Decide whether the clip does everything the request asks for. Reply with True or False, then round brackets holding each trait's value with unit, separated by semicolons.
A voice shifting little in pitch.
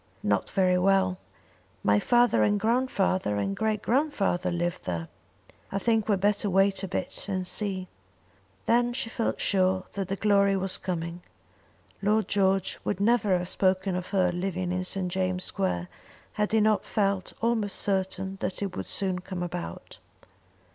True (2.1 semitones)